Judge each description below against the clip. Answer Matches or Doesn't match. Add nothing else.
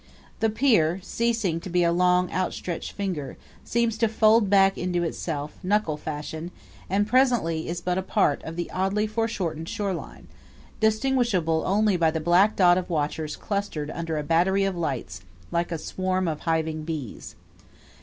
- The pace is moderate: Matches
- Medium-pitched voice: Matches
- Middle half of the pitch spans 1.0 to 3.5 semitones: Doesn't match